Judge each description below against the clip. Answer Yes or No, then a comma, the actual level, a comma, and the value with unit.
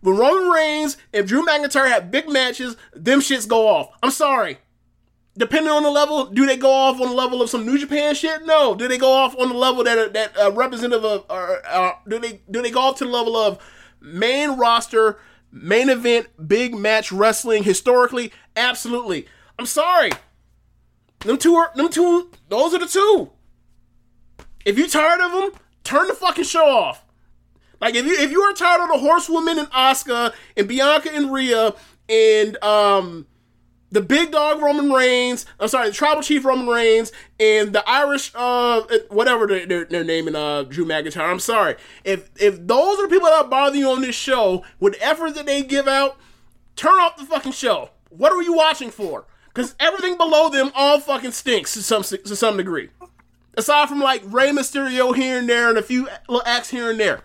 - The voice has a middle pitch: No, very high, 255 Hz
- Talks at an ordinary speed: Yes, average, 195 wpm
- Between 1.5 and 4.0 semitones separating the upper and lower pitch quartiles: No, average, 5.3 semitones